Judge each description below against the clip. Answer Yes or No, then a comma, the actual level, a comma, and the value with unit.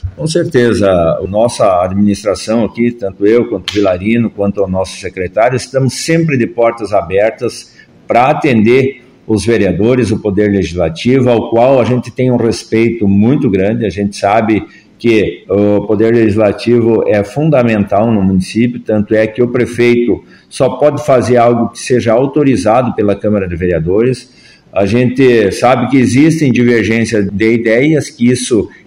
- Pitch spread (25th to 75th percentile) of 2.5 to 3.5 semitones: Yes, average, 3.2 semitones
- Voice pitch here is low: Yes, low, 115 Hz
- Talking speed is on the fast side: No, average, 150 wpm